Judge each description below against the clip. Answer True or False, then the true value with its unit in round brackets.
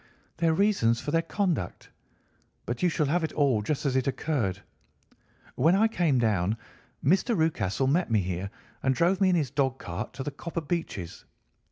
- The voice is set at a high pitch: False (145 Hz)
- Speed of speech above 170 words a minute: True (180 wpm)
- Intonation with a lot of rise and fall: True (6.4 semitones)